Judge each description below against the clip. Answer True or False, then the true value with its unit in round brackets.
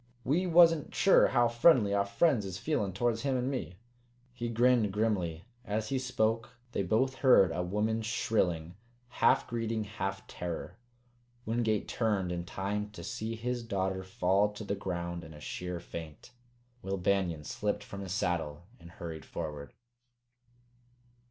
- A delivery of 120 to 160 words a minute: True (150 wpm)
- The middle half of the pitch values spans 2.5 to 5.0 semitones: True (4.7 semitones)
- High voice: False (105 Hz)